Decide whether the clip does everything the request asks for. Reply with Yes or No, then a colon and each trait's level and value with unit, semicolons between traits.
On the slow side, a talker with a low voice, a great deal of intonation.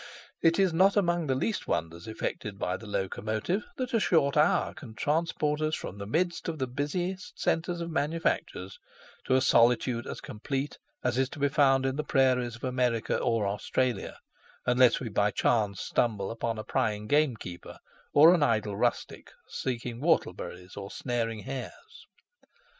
No: average, 165 wpm; low, 130 Hz; wide, 6.0 semitones